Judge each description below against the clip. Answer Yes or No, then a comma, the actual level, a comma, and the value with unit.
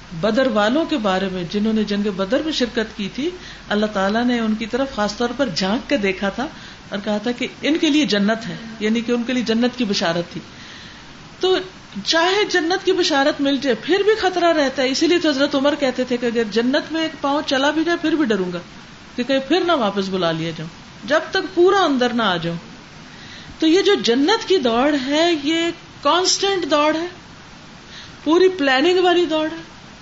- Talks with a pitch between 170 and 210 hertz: No, very high, 265 Hz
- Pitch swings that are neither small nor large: No, wide, 7.0 semitones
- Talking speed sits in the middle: No, fast, 210 wpm